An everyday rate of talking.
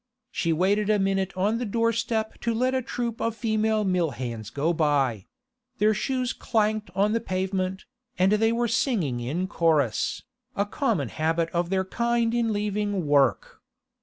Yes: average, 165 wpm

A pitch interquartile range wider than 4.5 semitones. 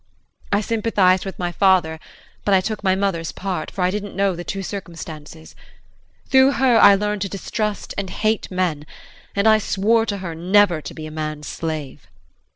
No: average, 3.6 semitones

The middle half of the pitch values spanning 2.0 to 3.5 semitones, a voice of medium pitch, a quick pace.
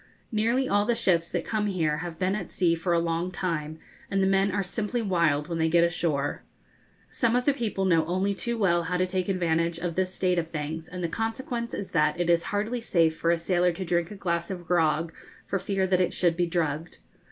Yes: average, 2.8 semitones; medium, 180 Hz; fast, 230 wpm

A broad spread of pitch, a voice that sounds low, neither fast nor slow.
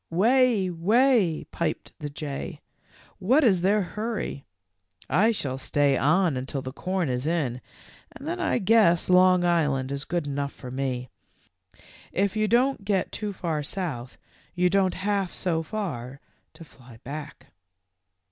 No: wide, 6.4 semitones; medium, 175 Hz; average, 145 wpm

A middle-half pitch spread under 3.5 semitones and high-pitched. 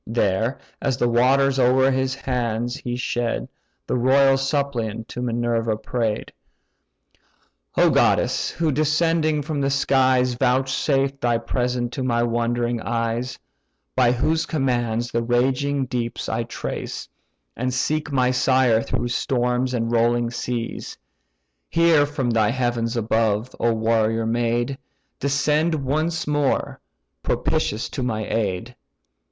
No: narrow, 2.5 semitones; low, 125 Hz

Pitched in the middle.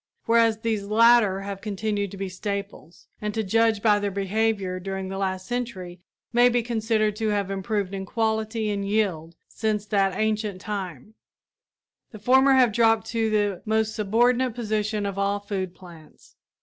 No: high, 210 Hz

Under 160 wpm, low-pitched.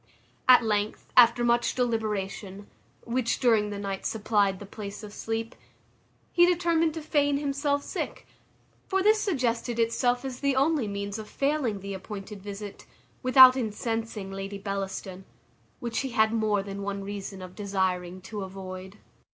No: average, 150 wpm; high, 220 Hz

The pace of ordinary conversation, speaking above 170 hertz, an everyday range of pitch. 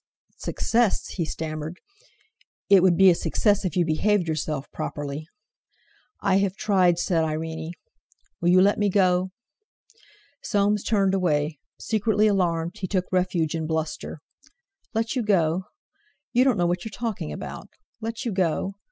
Yes: average, 145 wpm; medium, 185 Hz; average, 4.2 semitones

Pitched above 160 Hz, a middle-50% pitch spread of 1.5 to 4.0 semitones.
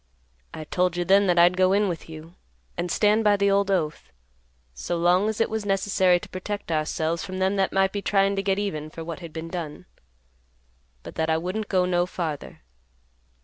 Yes: medium, 185 Hz; average, 3.0 semitones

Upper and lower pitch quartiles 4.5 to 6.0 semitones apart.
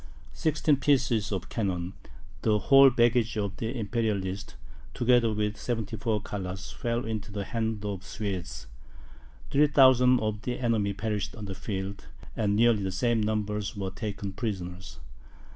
No: average, 3.0 semitones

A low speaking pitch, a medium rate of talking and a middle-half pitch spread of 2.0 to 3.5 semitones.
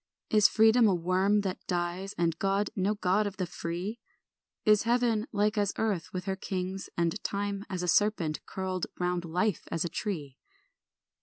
No: high, 190 Hz; average, 170 wpm; average, 2.8 semitones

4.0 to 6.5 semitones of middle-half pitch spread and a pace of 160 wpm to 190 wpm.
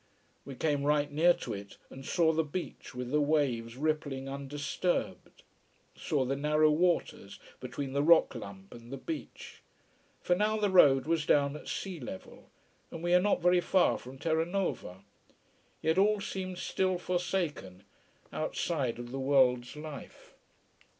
No: average, 4.8 semitones; average, 150 wpm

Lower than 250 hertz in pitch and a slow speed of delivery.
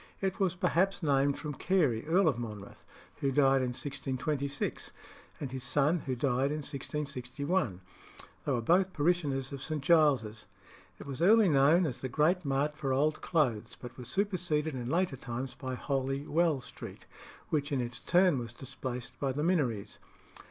No: medium, 140 Hz; average, 165 wpm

